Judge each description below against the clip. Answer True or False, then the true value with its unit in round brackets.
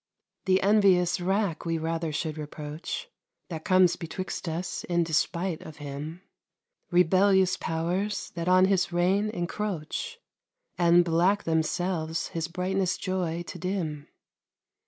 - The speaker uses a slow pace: True (120 wpm)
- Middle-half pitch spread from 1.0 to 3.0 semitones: True (2.6 semitones)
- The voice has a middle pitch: True (175 Hz)